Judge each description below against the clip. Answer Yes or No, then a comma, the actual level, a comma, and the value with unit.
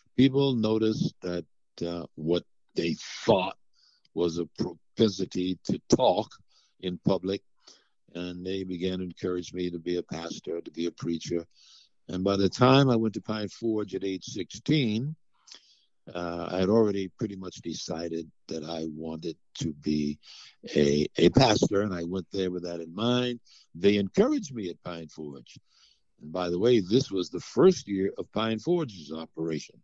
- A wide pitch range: No, average, 4.3 semitones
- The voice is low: Yes, very low, 90 Hz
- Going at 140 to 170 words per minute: Yes, average, 165 wpm